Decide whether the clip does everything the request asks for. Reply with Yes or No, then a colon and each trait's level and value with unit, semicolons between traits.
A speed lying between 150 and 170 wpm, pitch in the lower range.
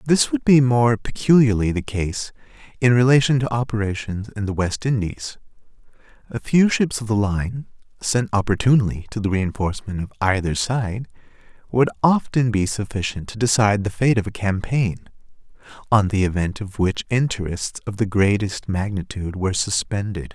Yes: average, 155 wpm; low, 110 Hz